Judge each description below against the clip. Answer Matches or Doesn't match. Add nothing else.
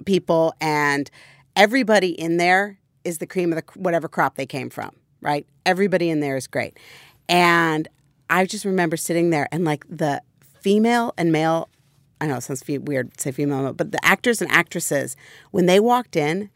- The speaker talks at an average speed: Matches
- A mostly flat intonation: Doesn't match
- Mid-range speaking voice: Matches